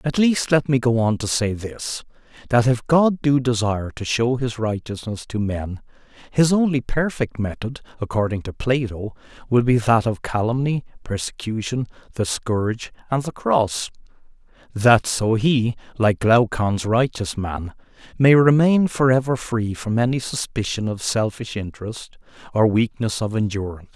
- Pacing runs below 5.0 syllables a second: Yes, 4.6 syllables/s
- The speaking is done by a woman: No, male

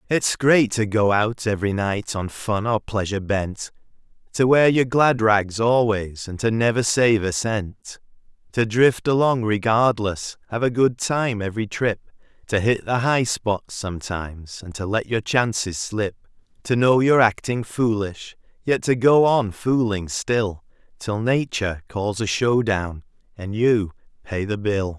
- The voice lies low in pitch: Yes, low, 110 Hz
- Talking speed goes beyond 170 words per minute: No, average, 165 wpm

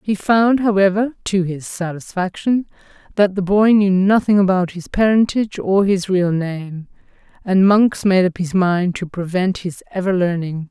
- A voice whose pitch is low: No, high, 190 Hz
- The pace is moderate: Yes, average, 160 wpm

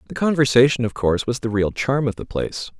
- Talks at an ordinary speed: No, fast, 235 wpm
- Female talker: No, male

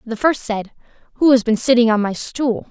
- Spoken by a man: No, female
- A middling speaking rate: No, fast, 220 wpm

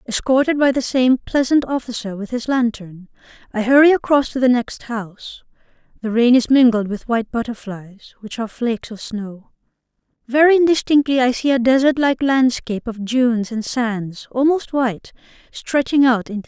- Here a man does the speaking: No, female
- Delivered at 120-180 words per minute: Yes, average, 170 wpm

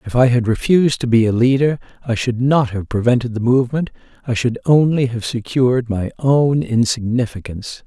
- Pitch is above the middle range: No, low, 125 Hz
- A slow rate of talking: No, average, 175 wpm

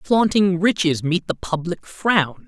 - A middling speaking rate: Yes, average, 145 wpm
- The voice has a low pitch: No, medium, 180 Hz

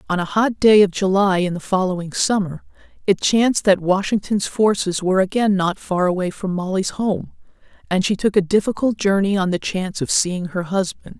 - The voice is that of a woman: Yes, female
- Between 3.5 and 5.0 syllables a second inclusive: No, 5.3 syllables/s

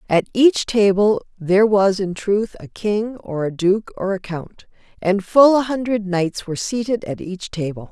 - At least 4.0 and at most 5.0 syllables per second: Yes, 4.4 syllables/s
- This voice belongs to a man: No, female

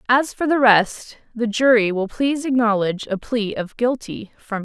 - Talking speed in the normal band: Yes, average, 180 wpm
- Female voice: Yes, female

